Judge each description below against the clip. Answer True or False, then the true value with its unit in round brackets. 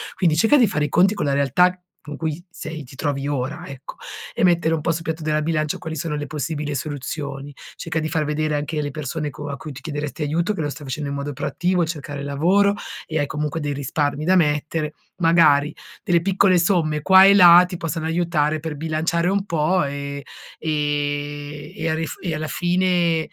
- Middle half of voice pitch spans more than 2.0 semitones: True (2.6 semitones)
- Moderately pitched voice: True (155 Hz)